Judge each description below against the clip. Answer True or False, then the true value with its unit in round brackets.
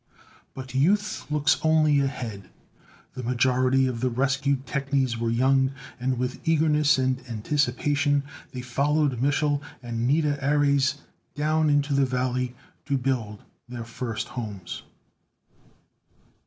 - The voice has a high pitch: False (135 Hz)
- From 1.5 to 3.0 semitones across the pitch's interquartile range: True (2.6 semitones)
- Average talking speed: False (120 wpm)